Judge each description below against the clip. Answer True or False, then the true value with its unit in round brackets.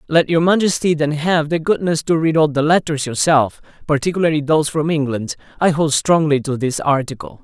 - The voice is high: False (150 Hz)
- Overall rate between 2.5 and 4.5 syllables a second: False (5.5 syllables/s)